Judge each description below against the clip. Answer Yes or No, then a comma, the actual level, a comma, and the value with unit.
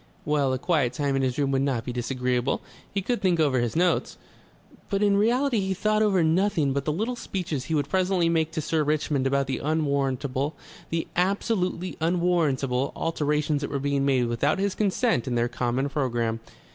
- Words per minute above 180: Yes, average, 190 wpm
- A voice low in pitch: No, medium, 150 Hz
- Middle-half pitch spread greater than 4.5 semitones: Yes, average, 5.2 semitones